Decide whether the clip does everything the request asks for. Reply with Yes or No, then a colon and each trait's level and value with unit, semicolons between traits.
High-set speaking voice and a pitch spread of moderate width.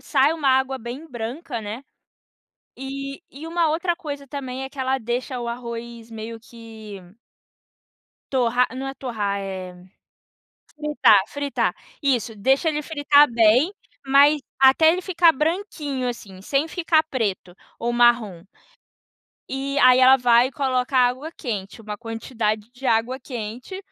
Yes: very high, 255 Hz; average, 3.8 semitones